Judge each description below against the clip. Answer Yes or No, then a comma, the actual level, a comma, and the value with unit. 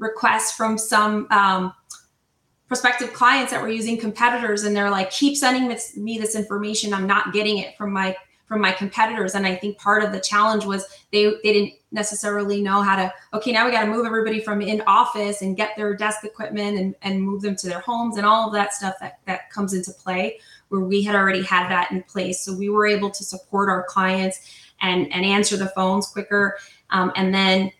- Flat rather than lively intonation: Yes, narrow, 1.9 semitones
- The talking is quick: Yes, fast, 215 wpm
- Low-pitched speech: No, high, 205 Hz